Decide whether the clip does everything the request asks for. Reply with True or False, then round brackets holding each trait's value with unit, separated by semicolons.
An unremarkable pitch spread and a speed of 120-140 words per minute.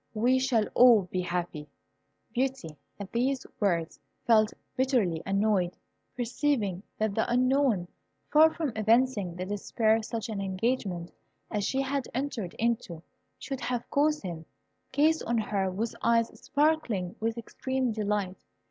True (5.0 semitones; 135 wpm)